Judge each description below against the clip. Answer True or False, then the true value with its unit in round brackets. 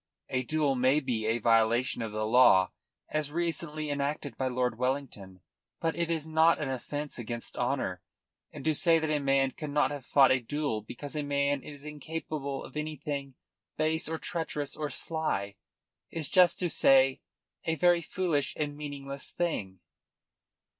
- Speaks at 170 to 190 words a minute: False (160 wpm)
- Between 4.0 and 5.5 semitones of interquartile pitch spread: False (3.3 semitones)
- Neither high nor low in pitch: True (145 Hz)